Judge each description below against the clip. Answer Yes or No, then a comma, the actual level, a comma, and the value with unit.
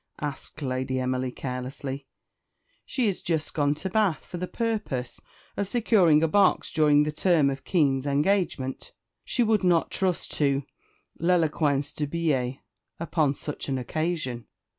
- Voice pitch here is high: No, medium, 150 Hz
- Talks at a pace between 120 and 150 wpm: Yes, average, 140 wpm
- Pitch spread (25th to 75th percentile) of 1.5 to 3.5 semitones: No, average, 4.7 semitones